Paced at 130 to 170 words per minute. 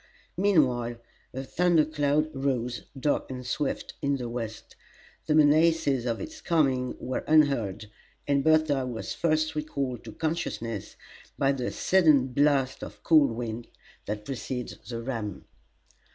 Yes: slow, 135 wpm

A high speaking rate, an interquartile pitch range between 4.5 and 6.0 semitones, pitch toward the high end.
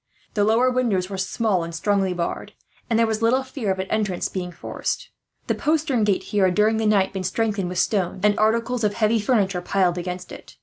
No: fast, 215 wpm; average, 3.3 semitones; high, 205 Hz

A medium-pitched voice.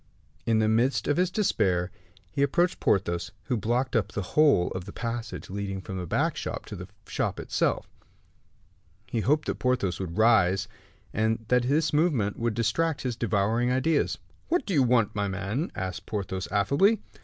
No: low, 115 Hz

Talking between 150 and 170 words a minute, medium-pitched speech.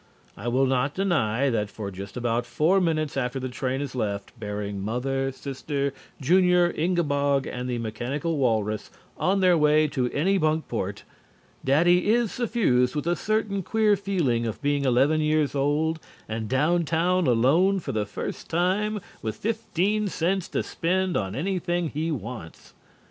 Yes: average, 155 wpm; medium, 145 Hz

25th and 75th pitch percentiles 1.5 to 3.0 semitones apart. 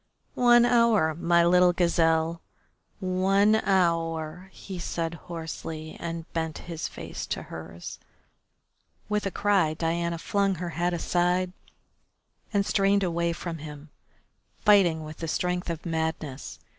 Yes: narrow, 2.5 semitones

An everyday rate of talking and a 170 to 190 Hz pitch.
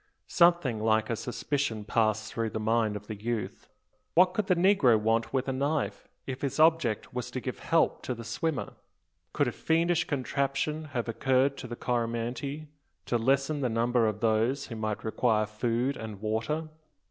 No: average, 175 wpm; low, 125 Hz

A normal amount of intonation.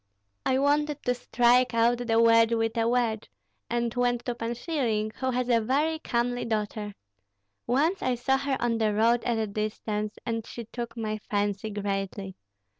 No: narrow, 2.3 semitones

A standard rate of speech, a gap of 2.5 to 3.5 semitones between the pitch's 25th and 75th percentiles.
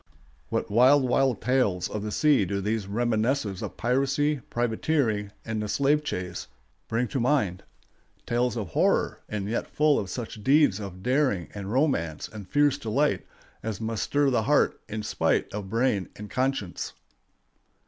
No: average, 155 wpm; average, 4.8 semitones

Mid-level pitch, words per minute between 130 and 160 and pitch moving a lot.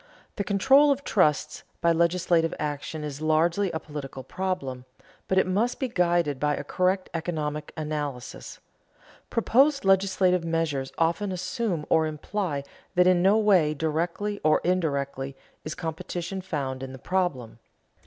No: medium, 170 Hz; average, 140 wpm; average, 4.0 semitones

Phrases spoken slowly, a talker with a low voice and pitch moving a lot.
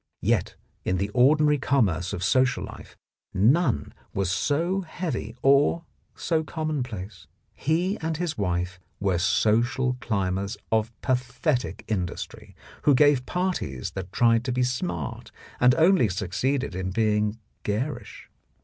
Yes: slow, 125 wpm; low, 125 Hz; wide, 6.9 semitones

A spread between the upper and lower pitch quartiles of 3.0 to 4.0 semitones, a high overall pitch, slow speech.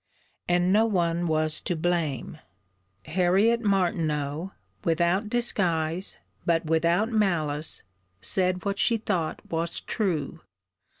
No: average, 3.5 semitones; medium, 175 Hz; slow, 105 wpm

